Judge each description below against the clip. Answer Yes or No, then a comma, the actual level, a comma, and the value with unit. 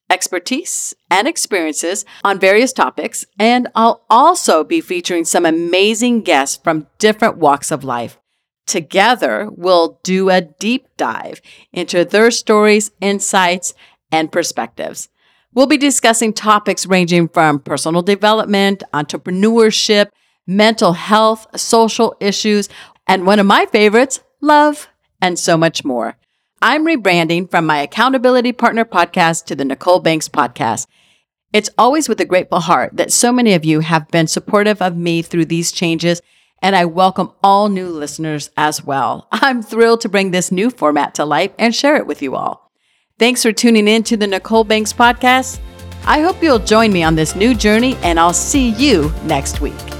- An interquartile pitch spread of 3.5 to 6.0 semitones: Yes, average, 5.0 semitones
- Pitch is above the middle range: Yes, high, 200 Hz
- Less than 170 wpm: Yes, average, 160 wpm